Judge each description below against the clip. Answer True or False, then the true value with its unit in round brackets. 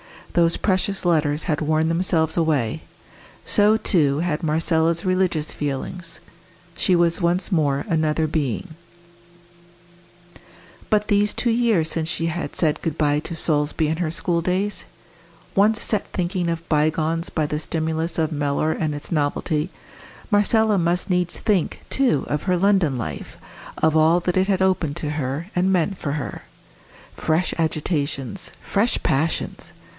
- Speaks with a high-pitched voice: False (165 Hz)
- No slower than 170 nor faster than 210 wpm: False (145 wpm)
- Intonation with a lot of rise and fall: False (3.1 semitones)